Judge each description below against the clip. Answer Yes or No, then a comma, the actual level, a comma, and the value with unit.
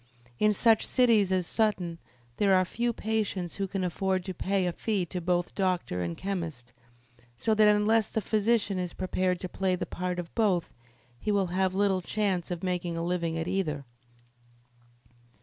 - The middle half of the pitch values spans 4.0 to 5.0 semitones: No, average, 2.9 semitones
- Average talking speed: Yes, average, 175 wpm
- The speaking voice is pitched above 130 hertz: Yes, medium, 185 Hz